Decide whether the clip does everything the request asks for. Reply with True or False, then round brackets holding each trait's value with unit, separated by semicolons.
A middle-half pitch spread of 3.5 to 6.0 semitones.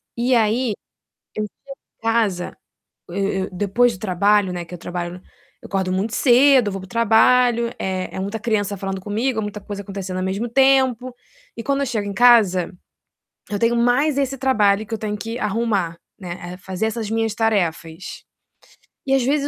True (3.8 semitones)